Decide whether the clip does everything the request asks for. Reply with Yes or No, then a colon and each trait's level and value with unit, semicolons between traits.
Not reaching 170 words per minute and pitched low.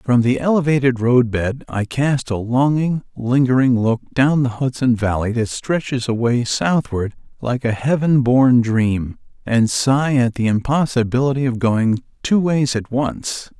Yes: average, 155 wpm; low, 125 Hz